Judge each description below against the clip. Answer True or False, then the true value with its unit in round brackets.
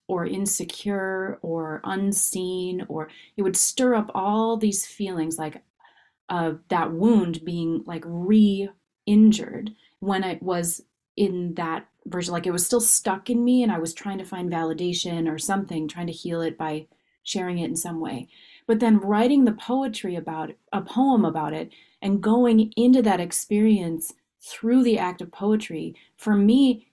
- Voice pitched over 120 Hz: True (190 Hz)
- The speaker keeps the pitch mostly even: False (4.2 semitones)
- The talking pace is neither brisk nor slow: True (165 wpm)